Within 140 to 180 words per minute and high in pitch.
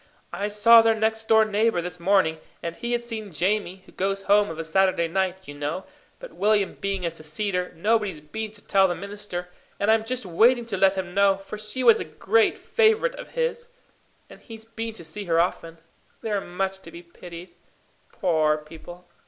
No: average, 195 wpm; high, 195 Hz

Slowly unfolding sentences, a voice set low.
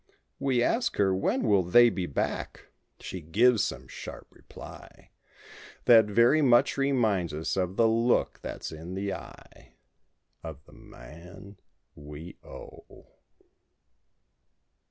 Yes: slow, 120 wpm; low, 100 Hz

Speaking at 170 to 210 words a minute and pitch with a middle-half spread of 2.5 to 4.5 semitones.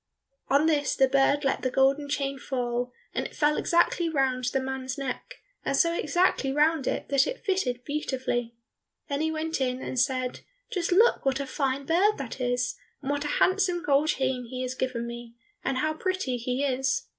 Yes: average, 190 wpm; average, 3.3 semitones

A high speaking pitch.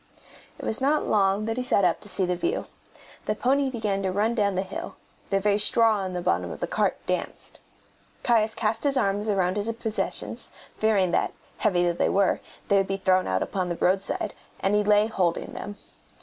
Yes: high, 205 Hz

